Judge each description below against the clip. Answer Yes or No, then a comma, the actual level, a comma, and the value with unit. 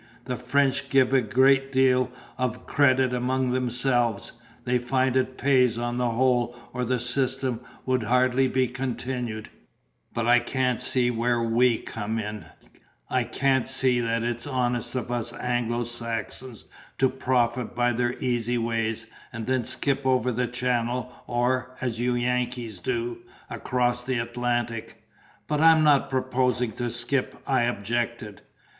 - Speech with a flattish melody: Yes, narrow, 1.4 semitones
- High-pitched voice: No, low, 125 Hz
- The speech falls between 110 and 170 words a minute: Yes, average, 145 wpm